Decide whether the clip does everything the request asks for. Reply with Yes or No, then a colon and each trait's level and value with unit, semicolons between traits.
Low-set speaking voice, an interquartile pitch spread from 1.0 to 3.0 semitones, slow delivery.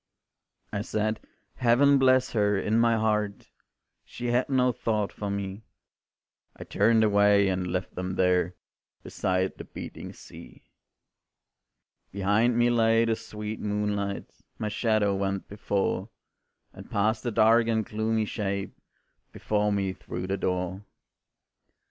Yes: low, 105 Hz; narrow, 2.4 semitones; slow, 130 wpm